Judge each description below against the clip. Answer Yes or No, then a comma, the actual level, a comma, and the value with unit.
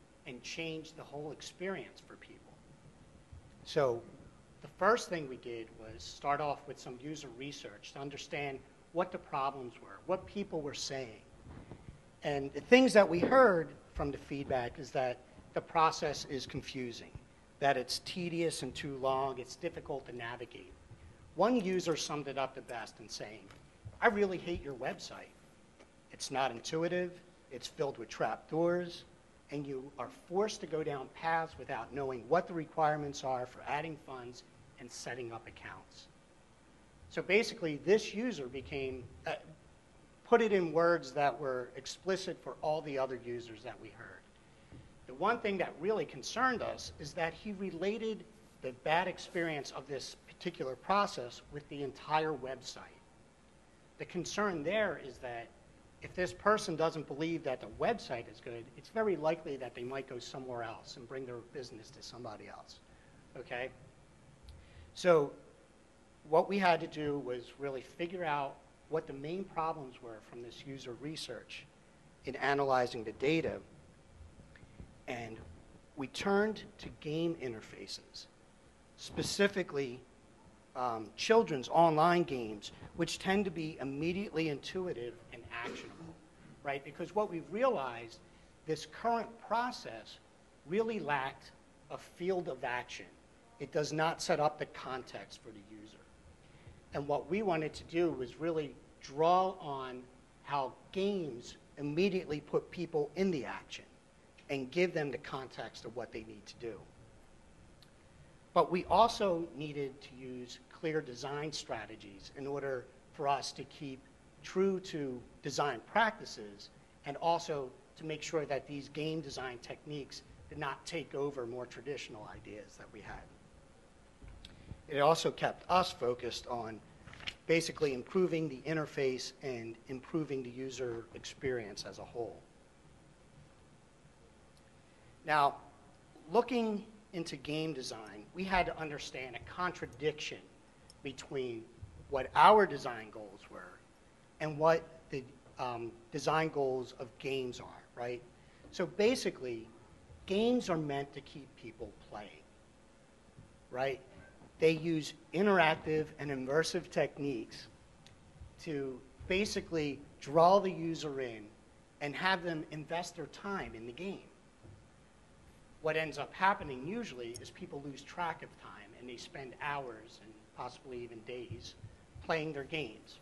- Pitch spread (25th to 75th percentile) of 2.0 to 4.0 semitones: No, average, 4.8 semitones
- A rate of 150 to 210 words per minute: No, average, 140 wpm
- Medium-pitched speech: Yes, medium, 145 Hz